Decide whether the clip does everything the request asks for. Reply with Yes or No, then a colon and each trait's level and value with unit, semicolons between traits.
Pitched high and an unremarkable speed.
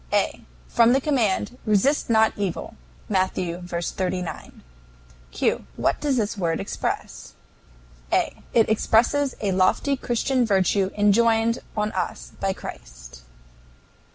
No: high, 205 Hz; slow, 120 wpm